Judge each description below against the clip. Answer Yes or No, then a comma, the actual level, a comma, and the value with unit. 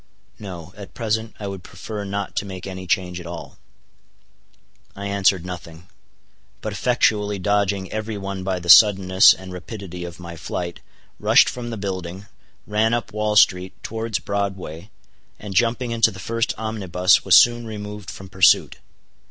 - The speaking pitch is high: No, low, 100 Hz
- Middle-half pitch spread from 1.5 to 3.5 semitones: Yes, average, 2.7 semitones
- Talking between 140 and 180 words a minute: Yes, average, 155 wpm